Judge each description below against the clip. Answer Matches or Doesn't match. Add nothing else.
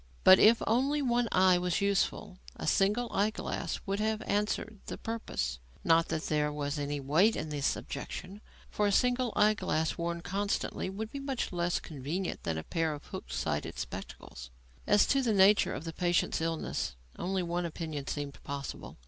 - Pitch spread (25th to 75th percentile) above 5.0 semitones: Matches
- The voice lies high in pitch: Doesn't match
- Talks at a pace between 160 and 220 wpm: Matches